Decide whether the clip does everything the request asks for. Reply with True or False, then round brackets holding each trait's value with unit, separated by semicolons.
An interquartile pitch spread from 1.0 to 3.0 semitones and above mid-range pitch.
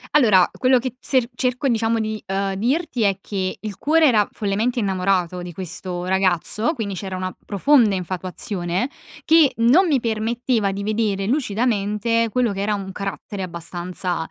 False (4.0 semitones; 205 Hz)